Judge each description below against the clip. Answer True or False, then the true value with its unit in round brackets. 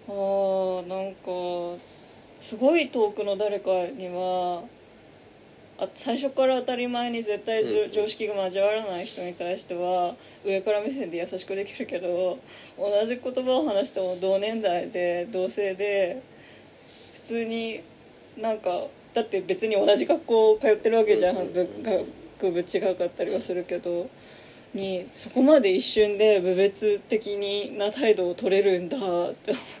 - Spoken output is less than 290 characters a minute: True (265 characters per minute)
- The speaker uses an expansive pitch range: False (3.4 semitones)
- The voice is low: False (200 Hz)